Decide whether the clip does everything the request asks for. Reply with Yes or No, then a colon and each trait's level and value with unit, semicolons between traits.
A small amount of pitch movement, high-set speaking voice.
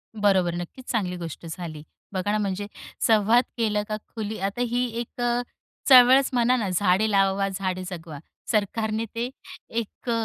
No: average, 3.6 semitones; high, 205 Hz